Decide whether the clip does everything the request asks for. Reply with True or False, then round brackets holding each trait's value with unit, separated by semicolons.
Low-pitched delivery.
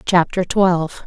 False (180 Hz)